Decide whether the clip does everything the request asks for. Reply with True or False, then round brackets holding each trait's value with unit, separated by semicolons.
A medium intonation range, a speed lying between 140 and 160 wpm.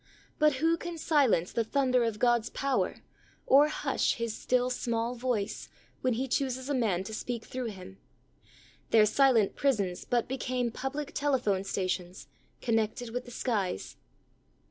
True (3.5 semitones; 150 wpm)